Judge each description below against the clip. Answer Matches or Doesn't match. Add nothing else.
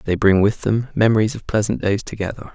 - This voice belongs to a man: Matches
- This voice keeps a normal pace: Doesn't match